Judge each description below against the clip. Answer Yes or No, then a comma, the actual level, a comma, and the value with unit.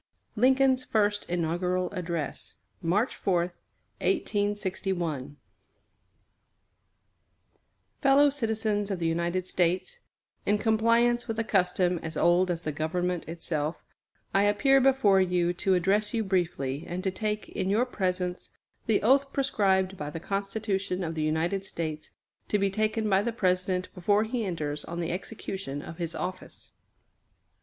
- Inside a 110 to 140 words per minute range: Yes, slow, 135 wpm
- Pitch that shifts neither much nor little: Yes, average, 3.7 semitones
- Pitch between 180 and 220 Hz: Yes, high, 190 Hz